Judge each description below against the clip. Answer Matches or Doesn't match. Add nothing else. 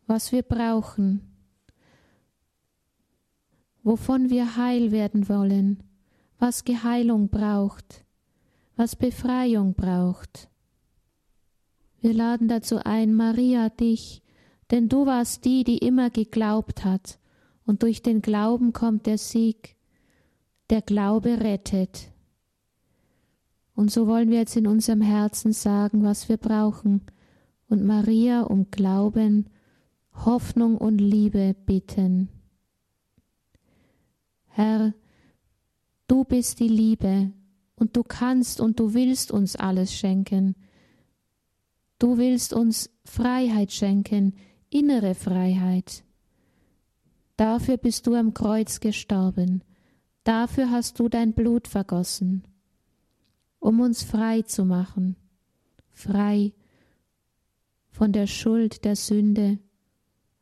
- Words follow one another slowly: Matches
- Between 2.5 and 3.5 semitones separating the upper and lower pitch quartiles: Matches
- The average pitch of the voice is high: Matches